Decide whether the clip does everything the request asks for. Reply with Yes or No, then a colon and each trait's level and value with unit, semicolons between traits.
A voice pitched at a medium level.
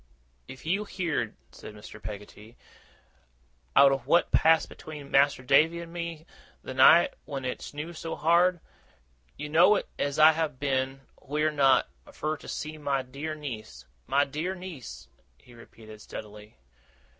Yes: medium, 145 Hz